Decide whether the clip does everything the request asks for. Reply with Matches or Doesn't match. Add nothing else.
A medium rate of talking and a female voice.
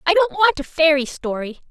Doesn't match